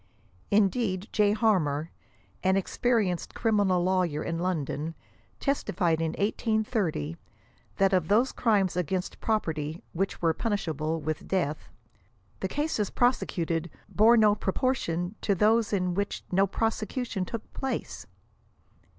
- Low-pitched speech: No, high, 190 Hz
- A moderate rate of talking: No, slow, 125 wpm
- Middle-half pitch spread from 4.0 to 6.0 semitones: Yes, average, 4.7 semitones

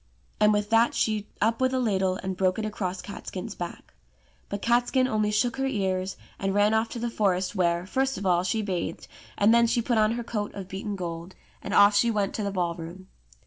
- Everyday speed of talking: No, fast, 225 wpm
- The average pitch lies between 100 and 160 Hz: No, high, 205 Hz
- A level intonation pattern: No, average, 3.3 semitones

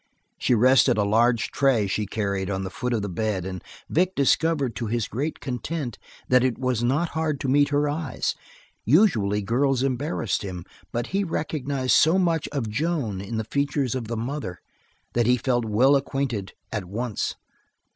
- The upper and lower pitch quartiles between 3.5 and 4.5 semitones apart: No, average, 4.9 semitones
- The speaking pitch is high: No, low, 125 Hz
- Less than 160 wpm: No, average, 175 wpm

